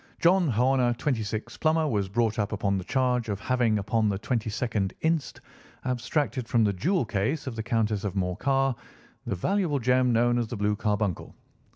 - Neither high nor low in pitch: No, low, 115 Hz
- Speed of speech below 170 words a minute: No, average, 175 wpm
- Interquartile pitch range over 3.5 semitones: Yes, average, 3.9 semitones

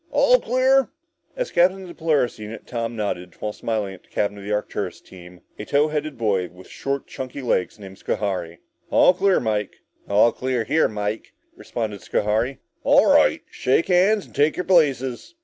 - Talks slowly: No, average, 185 wpm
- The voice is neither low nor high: No, low, 120 Hz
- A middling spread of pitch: No, wide, 7.6 semitones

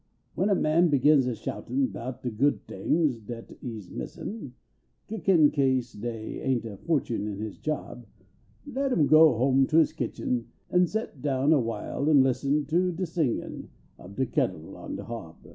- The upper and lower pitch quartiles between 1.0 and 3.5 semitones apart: No, average, 4.9 semitones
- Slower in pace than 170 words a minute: No, average, 185 wpm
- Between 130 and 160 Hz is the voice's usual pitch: Yes, low, 135 Hz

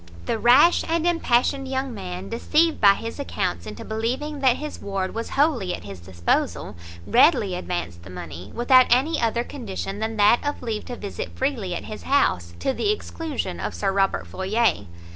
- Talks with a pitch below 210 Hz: No, high, 230 Hz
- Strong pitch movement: Yes, wide, 6.3 semitones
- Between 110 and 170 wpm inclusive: No, average, 180 wpm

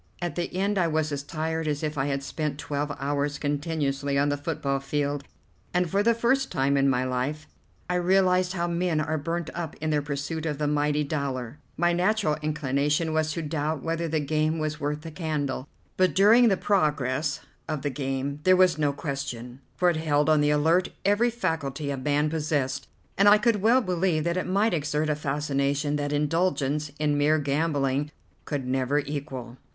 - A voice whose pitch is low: No, medium, 150 Hz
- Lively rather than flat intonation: No, average, 2.9 semitones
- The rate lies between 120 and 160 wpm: No, average, 190 wpm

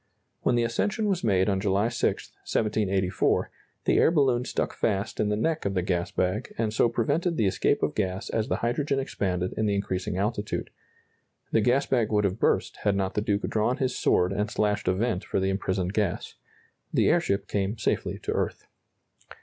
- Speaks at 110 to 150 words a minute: No, average, 195 wpm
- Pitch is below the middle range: Yes, low, 105 Hz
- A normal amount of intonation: Yes, average, 3.5 semitones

